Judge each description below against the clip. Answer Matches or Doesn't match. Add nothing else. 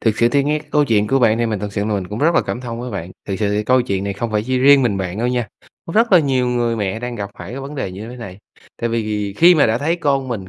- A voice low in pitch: Matches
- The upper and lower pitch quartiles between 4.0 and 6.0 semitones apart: Matches